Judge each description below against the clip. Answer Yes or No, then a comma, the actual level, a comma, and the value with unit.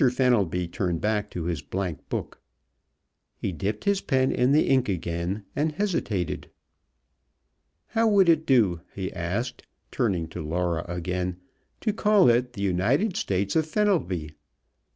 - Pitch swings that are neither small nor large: No, wide, 8.1 semitones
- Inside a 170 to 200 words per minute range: No, slow, 135 wpm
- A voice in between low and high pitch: No, low, 105 Hz